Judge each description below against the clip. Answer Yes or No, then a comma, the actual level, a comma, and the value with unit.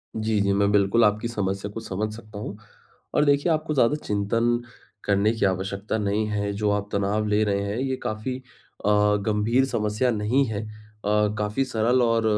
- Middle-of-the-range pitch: No, low, 105 Hz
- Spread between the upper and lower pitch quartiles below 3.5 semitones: Yes, narrow, 2.4 semitones